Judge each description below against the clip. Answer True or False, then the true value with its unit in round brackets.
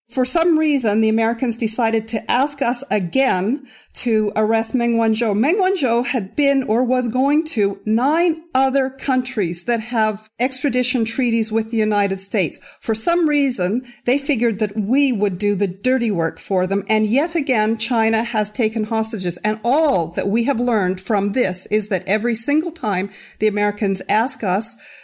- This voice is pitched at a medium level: False (225 Hz)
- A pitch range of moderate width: True (3.4 semitones)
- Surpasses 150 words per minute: True (170 wpm)